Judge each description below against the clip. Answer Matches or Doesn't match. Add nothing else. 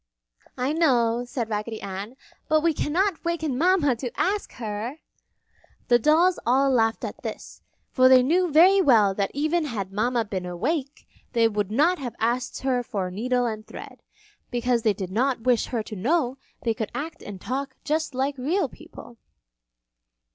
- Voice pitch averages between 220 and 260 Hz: Matches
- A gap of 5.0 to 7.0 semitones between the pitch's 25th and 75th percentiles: Matches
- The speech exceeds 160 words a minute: Matches